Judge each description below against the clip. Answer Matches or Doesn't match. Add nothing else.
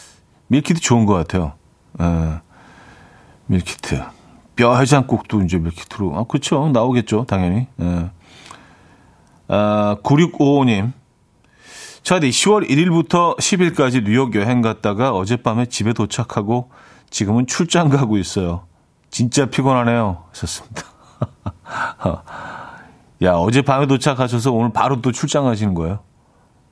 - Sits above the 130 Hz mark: Doesn't match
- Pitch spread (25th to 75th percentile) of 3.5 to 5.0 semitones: Doesn't match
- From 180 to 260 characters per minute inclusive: Matches